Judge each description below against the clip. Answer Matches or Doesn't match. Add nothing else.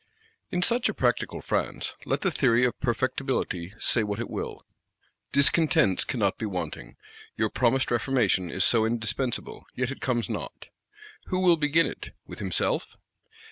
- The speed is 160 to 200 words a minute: Doesn't match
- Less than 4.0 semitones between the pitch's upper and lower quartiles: Doesn't match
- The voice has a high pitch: Doesn't match